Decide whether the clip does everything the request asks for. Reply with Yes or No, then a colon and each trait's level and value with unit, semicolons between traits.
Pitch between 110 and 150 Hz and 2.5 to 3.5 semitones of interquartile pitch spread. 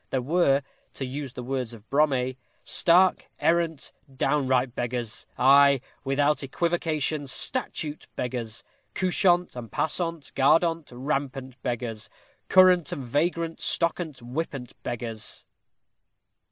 No: medium, 140 Hz; average, 4.6 semitones